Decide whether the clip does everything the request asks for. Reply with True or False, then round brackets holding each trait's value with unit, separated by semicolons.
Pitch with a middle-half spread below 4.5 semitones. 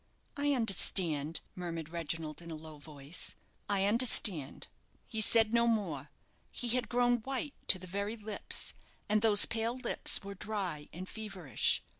False (5.5 semitones)